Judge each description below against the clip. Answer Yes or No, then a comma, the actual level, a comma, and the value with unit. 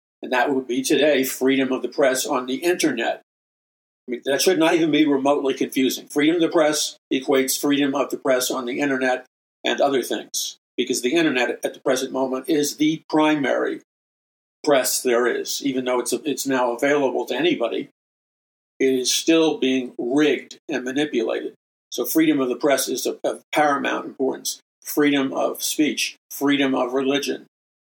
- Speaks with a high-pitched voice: No, medium, 140 Hz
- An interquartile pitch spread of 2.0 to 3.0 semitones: Yes, average, 2.7 semitones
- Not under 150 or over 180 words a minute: Yes, average, 175 wpm